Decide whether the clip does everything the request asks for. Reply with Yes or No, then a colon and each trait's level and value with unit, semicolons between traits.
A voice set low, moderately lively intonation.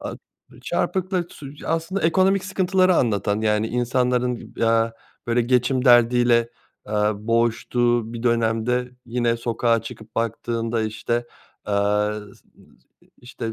No: low, 120 Hz; narrow, 1.8 semitones